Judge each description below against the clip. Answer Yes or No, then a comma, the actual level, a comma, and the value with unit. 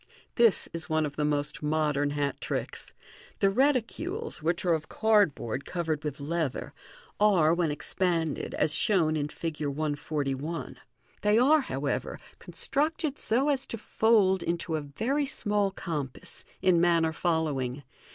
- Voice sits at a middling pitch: Yes, medium, 165 Hz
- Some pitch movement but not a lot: No, wide, 5.9 semitones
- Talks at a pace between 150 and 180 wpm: No, average, 140 wpm